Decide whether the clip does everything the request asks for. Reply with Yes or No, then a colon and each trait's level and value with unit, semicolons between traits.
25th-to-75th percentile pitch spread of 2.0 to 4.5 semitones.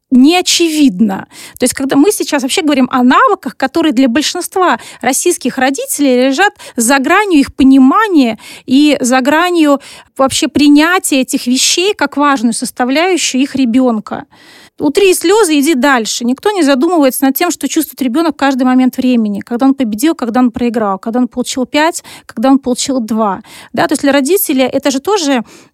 Yes: average, 3.8 semitones